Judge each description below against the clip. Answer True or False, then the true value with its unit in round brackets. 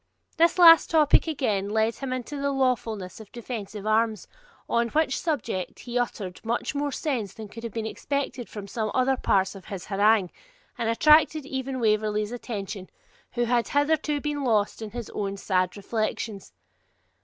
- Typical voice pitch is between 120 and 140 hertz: False (230 Hz)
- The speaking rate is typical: True (165 wpm)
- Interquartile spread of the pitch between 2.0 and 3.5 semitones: False (4.4 semitones)